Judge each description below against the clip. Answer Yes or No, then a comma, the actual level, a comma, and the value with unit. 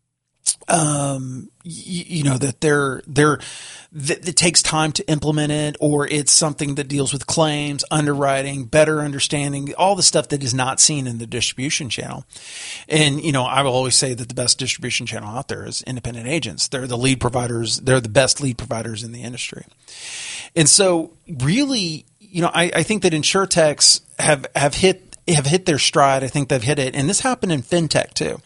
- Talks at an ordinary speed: Yes, average, 195 wpm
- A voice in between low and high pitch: Yes, medium, 145 Hz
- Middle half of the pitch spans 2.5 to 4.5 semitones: Yes, average, 3.6 semitones